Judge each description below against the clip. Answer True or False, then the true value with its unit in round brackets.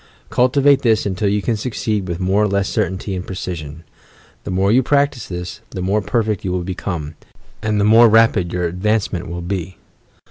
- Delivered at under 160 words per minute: False (185 wpm)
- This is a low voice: True (100 Hz)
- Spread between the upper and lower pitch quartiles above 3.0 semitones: True (3.5 semitones)